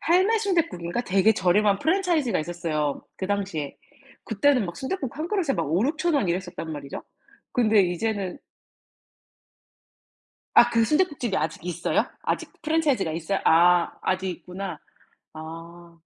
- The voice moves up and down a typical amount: No, wide, 8.7 semitones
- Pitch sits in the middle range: No, high, 195 Hz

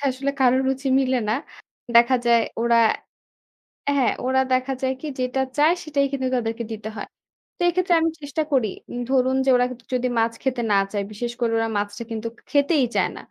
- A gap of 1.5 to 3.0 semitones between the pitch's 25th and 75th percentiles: Yes, average, 2.7 semitones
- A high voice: Yes, very high, 255 Hz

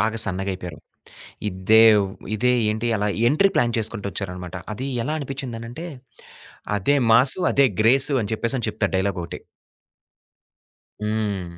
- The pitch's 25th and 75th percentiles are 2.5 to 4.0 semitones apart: No, average, 4.4 semitones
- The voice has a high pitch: No, low, 110 Hz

